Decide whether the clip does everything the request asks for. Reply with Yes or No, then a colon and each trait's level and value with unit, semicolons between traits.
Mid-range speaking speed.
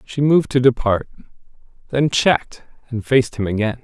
Yes: average, 155 wpm